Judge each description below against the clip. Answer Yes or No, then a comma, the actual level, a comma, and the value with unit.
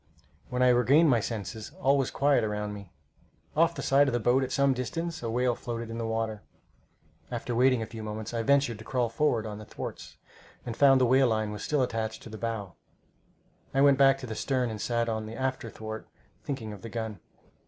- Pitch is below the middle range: Yes, low, 120 Hz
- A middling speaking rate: No, fast, 220 wpm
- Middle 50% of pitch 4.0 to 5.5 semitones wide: No, average, 3.3 semitones